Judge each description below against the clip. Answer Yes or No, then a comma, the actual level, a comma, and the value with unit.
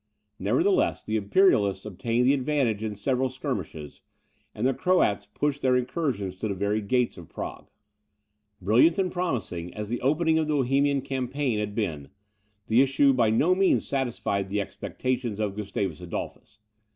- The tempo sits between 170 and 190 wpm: No, average, 155 wpm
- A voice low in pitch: Yes, low, 120 Hz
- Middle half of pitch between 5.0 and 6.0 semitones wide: Yes, wide, 5.4 semitones